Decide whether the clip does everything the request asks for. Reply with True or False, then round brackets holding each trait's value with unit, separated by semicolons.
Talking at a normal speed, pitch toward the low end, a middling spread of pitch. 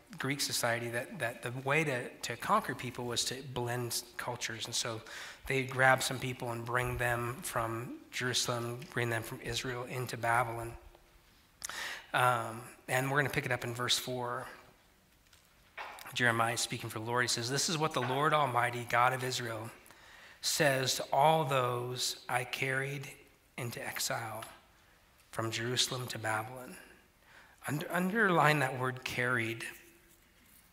False (150 wpm; 125 Hz; 1.8 semitones)